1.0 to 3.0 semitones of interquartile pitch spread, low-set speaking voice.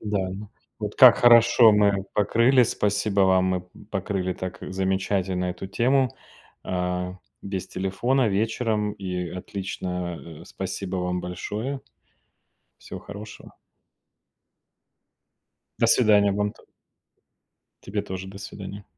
Yes: narrow, 2.4 semitones; low, 100 Hz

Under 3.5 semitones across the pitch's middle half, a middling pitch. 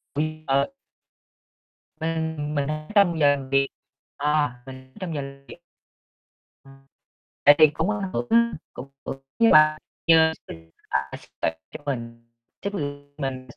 Yes: average, 2.9 semitones; medium, 145 Hz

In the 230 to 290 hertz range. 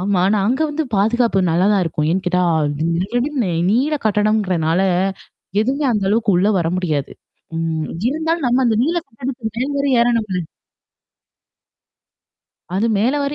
No: high, 215 Hz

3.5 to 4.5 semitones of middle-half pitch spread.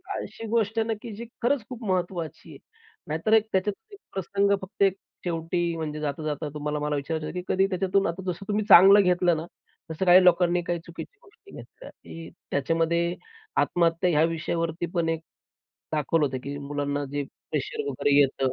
Yes: average, 3.9 semitones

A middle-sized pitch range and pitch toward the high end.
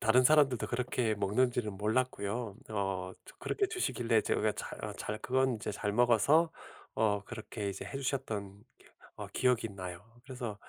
No: average, 3.7 semitones; low, 110 Hz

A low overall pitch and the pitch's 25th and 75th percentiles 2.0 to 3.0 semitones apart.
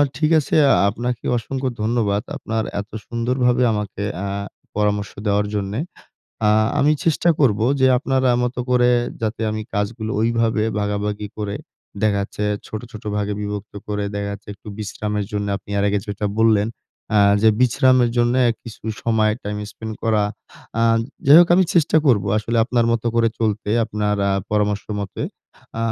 Yes: low, 110 Hz; narrow, 2.5 semitones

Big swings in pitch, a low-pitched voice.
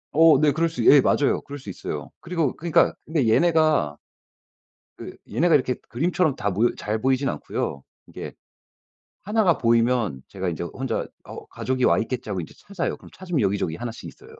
Yes: wide, 6.6 semitones; low, 130 Hz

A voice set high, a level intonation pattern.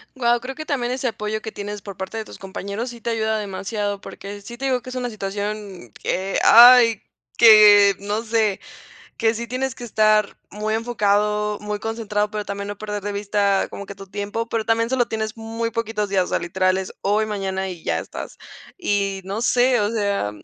Yes: high, 210 Hz; narrow, 2.3 semitones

